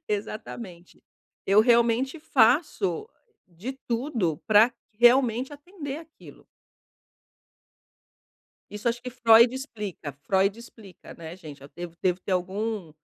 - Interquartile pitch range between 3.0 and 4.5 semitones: No, average, 5.2 semitones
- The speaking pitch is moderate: No, high, 220 Hz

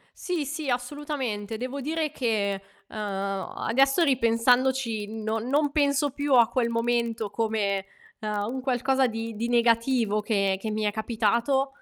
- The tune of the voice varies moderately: Yes, average, 3.7 semitones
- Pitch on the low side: No, high, 235 Hz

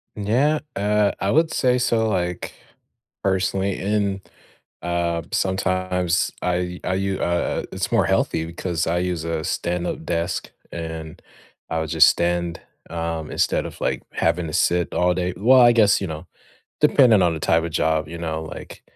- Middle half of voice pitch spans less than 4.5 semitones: Yes, average, 2.9 semitones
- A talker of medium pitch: No, very low, 90 Hz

